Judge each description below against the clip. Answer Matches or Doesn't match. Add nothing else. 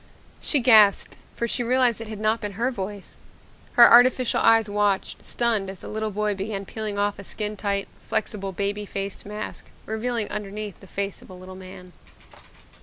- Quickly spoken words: Doesn't match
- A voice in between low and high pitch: Doesn't match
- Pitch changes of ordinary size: Doesn't match